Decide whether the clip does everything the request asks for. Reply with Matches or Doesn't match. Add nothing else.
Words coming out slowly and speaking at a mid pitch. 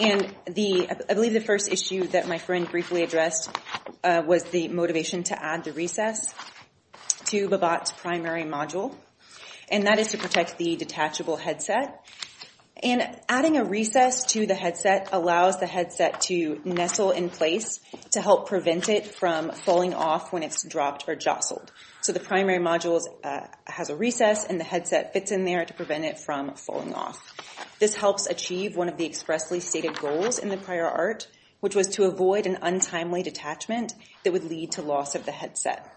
Doesn't match